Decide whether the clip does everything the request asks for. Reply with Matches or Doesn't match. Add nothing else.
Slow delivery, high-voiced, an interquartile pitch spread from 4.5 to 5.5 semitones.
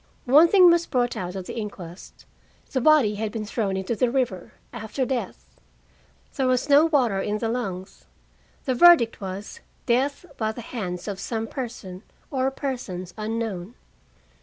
Doesn't match